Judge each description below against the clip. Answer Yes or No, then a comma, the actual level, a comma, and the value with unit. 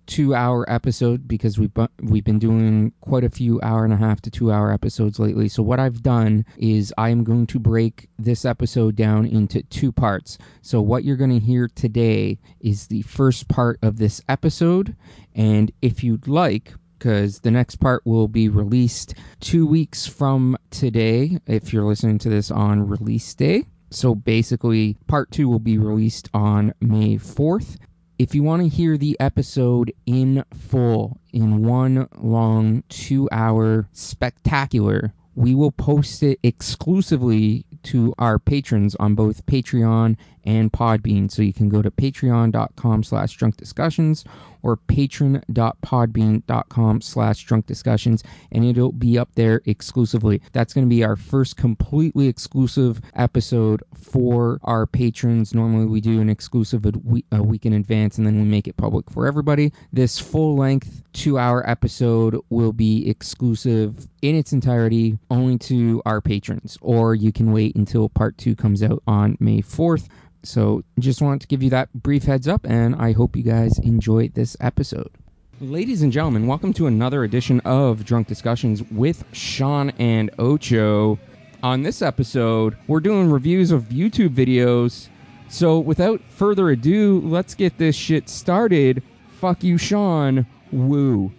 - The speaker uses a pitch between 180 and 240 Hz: No, low, 120 Hz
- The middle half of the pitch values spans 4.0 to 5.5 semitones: No, average, 3.5 semitones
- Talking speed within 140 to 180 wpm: Yes, average, 160 wpm